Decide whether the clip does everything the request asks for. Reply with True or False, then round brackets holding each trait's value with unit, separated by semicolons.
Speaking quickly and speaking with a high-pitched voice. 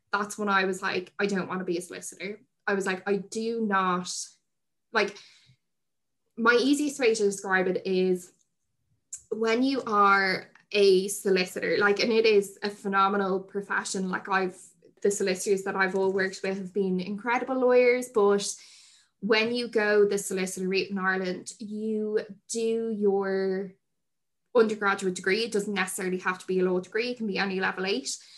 False (165 wpm; 200 Hz)